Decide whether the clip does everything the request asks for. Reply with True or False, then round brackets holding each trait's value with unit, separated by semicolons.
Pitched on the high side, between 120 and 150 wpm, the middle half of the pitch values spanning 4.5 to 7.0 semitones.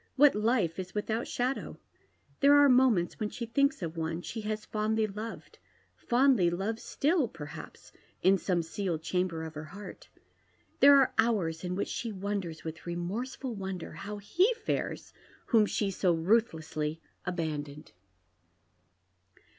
True (200 Hz; 145 wpm; 5.5 semitones)